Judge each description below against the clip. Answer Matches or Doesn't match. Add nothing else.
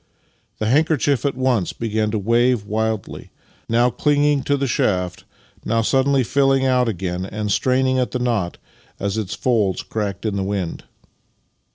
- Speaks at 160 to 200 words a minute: Matches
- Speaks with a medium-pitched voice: Doesn't match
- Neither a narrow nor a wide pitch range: Matches